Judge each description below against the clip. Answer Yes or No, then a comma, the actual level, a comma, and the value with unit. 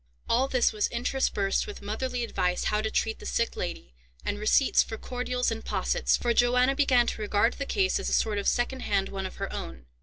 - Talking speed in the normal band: No, fast, 215 wpm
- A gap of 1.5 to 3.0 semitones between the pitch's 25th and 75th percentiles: No, average, 3.5 semitones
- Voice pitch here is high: Yes, high, 235 Hz